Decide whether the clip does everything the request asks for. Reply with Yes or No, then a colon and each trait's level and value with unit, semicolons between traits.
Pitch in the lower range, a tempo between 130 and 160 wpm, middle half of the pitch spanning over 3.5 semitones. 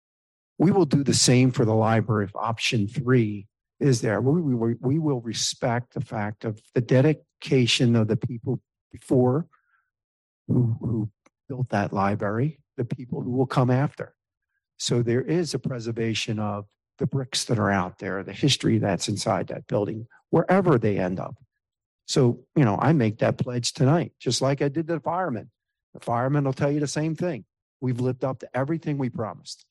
No: low, 125 Hz; average, 180 wpm; average, 4.2 semitones